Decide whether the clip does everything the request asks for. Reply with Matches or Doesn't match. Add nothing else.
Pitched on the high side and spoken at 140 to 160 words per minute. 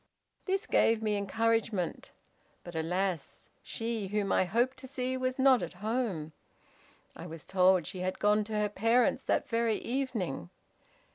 Matches